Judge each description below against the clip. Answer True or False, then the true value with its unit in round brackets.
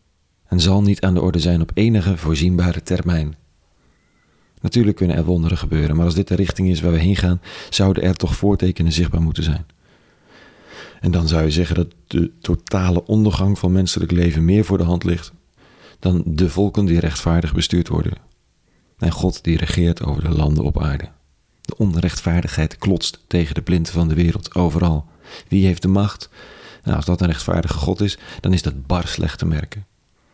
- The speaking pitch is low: True (85 Hz)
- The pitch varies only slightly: True (2.2 semitones)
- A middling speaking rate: True (185 wpm)